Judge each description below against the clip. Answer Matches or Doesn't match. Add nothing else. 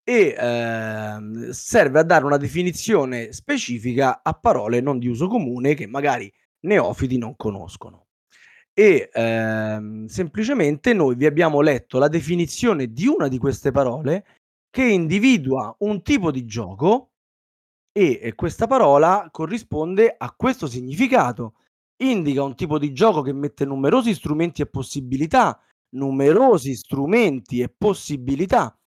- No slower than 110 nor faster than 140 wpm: Matches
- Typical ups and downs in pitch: Doesn't match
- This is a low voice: Doesn't match